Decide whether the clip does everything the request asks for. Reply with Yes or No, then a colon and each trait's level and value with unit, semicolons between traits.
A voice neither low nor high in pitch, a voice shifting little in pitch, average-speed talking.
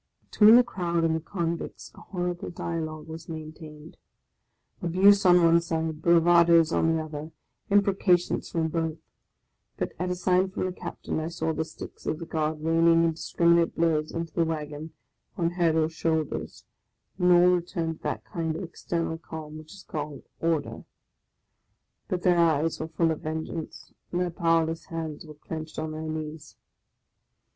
Yes: medium, 165 Hz; narrow, 1.5 semitones; average, 170 wpm